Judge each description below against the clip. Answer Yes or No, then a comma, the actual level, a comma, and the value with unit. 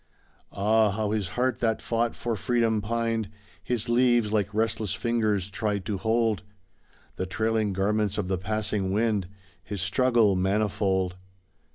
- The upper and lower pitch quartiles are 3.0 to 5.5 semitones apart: No, narrow, 2.4 semitones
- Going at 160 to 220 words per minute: No, average, 140 wpm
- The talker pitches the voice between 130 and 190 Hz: No, low, 110 Hz